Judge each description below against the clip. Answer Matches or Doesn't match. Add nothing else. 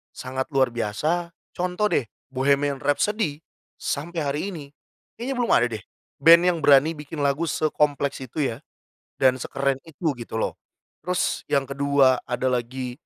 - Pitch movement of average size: Matches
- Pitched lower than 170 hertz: Matches